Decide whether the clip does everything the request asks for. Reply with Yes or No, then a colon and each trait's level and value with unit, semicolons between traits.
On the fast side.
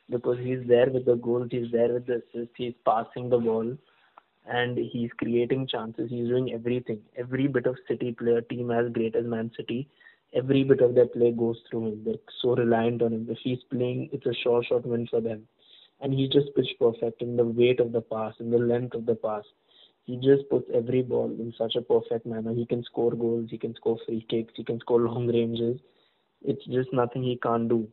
Yes: fast, 220 wpm